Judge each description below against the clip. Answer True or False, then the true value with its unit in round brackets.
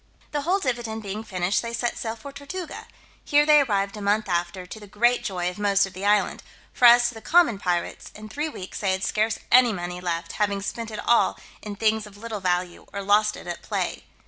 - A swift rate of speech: True (225 wpm)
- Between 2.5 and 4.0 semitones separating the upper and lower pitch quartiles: True (3.6 semitones)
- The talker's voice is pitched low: False (210 Hz)